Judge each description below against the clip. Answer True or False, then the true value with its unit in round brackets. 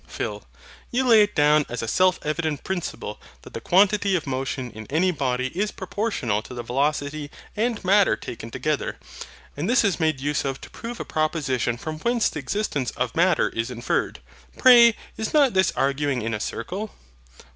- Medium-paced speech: True (180 wpm)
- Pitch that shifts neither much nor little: False (7.6 semitones)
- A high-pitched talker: False (155 Hz)